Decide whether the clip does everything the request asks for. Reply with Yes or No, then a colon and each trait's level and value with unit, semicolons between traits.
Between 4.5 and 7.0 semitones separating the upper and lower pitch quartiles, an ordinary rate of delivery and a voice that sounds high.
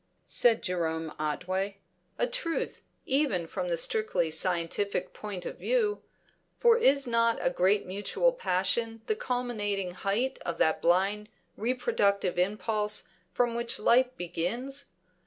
No: wide, 5.4 semitones; slow, 125 wpm; high, 210 Hz